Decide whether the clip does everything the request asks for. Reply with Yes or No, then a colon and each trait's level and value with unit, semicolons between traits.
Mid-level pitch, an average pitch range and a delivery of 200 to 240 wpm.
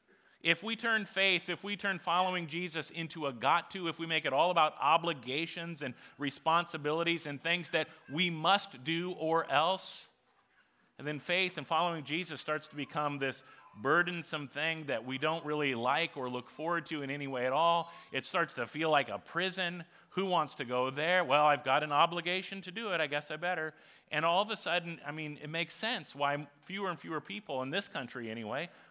Yes: medium, 160 Hz; average, 3.2 semitones; fast, 205 wpm